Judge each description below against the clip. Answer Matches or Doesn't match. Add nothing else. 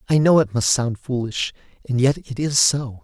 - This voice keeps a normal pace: Doesn't match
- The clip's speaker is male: Matches